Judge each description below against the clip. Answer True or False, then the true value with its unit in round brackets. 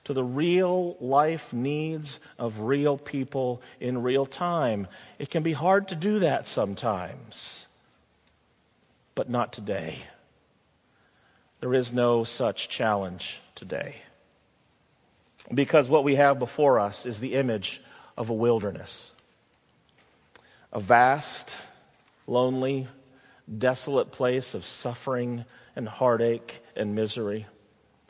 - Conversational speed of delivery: False (110 wpm)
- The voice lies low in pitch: True (125 Hz)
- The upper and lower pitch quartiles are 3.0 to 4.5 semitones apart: True (3.5 semitones)